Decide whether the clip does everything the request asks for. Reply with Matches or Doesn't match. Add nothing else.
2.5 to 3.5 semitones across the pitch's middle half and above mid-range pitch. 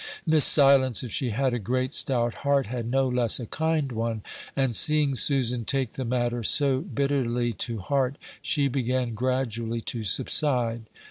Doesn't match